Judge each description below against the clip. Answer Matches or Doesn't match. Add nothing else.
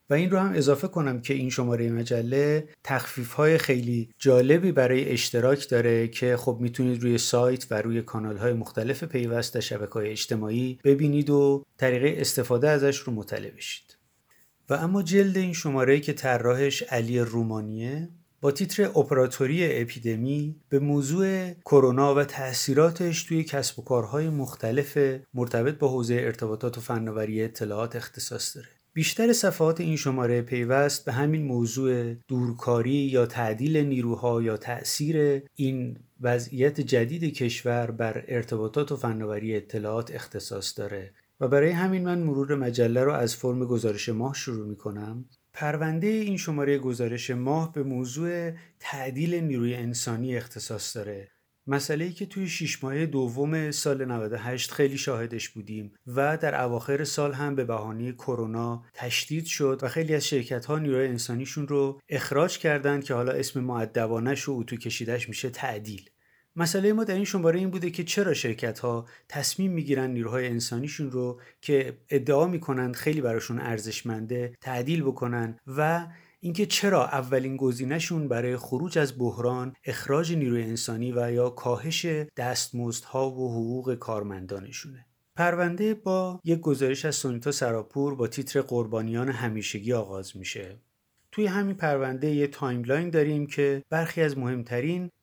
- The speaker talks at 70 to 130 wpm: Doesn't match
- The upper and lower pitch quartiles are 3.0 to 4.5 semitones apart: Matches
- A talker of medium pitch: Doesn't match